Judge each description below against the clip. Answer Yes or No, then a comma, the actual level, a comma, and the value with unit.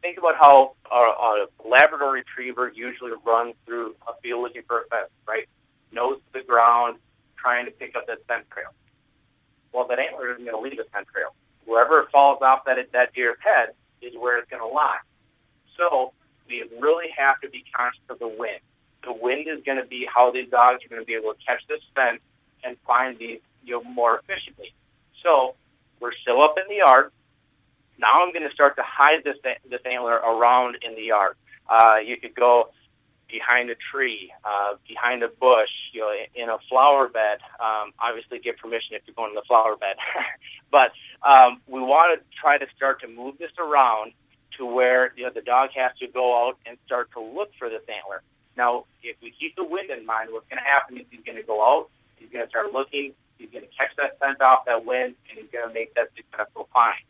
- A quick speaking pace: Yes, fast, 215 wpm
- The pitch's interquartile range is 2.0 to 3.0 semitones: Yes, average, 2.7 semitones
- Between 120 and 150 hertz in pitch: Yes, low, 125 Hz